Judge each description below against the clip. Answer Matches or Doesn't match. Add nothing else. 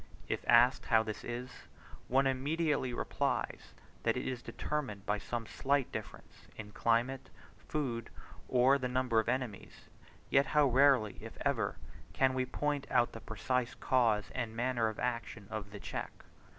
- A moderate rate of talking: Matches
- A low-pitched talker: Matches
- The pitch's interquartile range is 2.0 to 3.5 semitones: Matches